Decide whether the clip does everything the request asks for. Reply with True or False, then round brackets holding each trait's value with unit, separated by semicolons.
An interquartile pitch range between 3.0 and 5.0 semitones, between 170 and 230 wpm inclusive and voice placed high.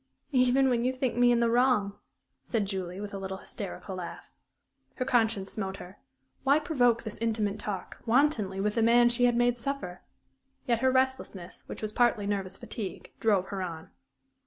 True (3.9 semitones; 180 wpm; 225 Hz)